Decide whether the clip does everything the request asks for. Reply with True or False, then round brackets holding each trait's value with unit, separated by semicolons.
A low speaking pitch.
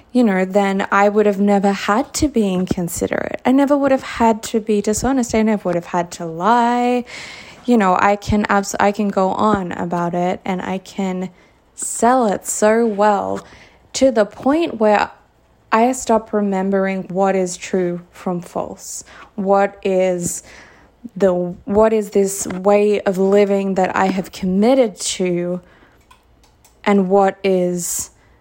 False (200 Hz)